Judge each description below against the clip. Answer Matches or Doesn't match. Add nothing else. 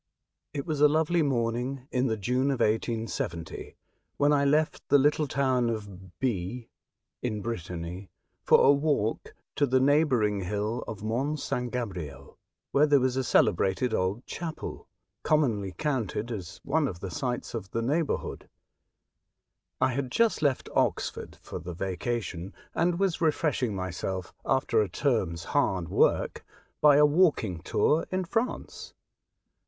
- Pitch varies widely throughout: Matches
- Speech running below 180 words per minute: Matches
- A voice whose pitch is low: Matches